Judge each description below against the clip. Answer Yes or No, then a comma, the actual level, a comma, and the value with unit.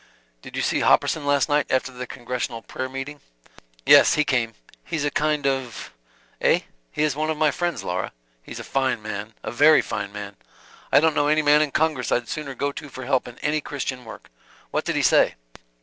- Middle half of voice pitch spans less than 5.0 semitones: Yes, average, 3.5 semitones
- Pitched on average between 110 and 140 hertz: Yes, low, 135 Hz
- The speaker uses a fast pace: Yes, fast, 210 wpm